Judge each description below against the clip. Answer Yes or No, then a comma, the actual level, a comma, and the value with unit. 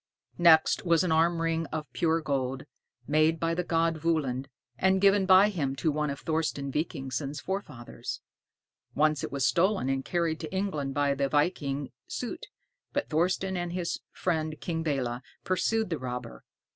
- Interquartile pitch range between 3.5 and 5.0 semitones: Yes, average, 3.9 semitones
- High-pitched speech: No, medium, 160 Hz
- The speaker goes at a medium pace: Yes, average, 160 wpm